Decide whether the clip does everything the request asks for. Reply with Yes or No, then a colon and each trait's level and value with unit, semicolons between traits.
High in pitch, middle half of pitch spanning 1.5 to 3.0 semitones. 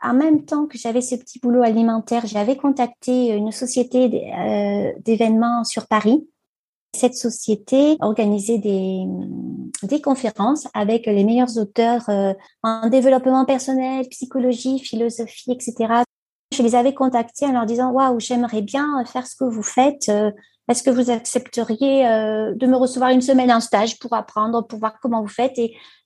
Yes: high, 240 Hz; narrow, 2.5 semitones